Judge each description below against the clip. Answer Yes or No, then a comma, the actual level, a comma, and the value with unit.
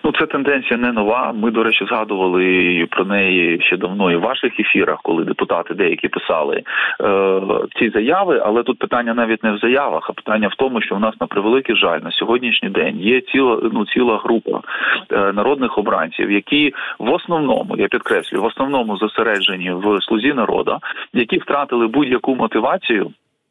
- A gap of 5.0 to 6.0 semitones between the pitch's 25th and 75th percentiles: No, average, 4.0 semitones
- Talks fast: Yes, fast, 170 wpm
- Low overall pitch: Yes, low, 115 Hz